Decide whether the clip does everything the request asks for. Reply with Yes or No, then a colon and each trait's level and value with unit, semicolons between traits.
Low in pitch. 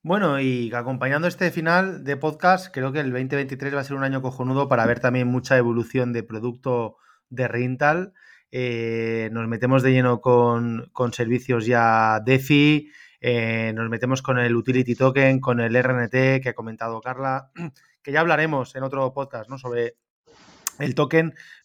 Yes: low, 130 Hz